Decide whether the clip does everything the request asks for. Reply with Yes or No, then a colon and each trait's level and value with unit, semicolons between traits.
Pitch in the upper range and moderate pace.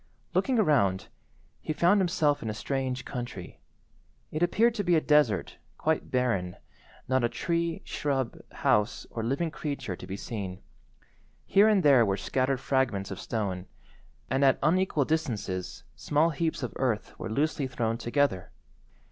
No: low, 130 Hz; average, 150 wpm